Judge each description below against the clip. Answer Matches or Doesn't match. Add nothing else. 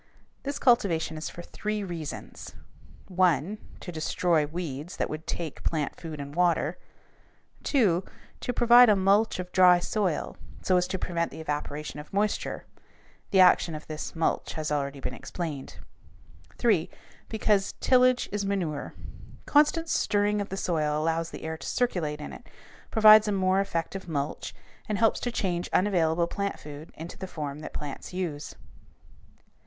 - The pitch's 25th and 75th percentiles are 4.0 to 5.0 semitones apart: Matches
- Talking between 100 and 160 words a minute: Matches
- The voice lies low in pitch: Doesn't match